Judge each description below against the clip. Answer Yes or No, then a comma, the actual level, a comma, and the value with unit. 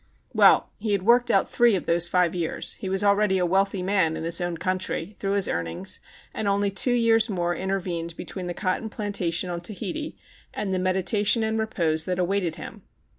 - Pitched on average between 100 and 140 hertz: No, high, 190 Hz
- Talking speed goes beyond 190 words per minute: Yes, average, 200 wpm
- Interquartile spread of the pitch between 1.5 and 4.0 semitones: Yes, average, 2.9 semitones